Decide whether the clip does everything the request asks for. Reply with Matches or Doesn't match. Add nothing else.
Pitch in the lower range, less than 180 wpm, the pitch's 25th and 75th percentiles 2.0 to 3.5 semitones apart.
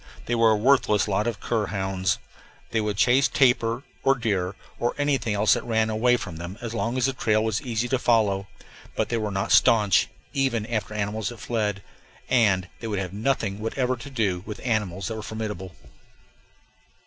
Doesn't match